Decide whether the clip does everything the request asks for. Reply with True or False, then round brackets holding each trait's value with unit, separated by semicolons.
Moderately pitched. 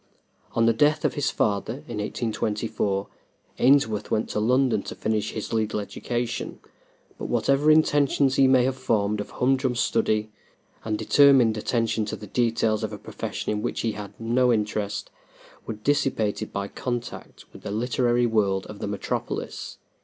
False (115 Hz)